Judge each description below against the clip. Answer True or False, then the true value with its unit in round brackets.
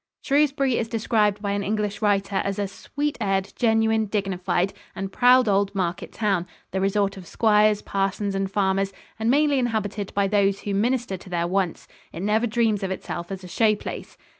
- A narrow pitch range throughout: True (2.3 semitones)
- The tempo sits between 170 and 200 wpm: True (185 wpm)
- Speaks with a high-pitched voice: True (205 Hz)